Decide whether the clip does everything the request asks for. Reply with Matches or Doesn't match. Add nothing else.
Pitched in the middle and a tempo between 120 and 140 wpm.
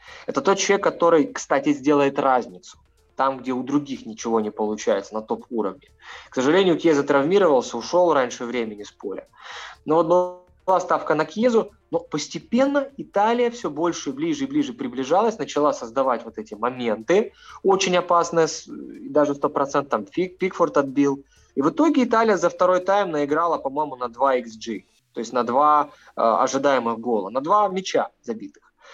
Doesn't match